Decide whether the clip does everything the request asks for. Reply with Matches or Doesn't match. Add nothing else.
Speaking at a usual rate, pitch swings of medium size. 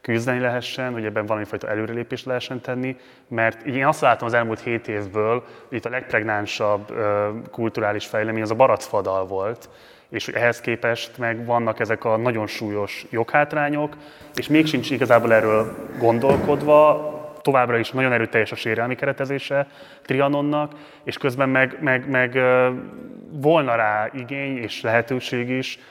Matches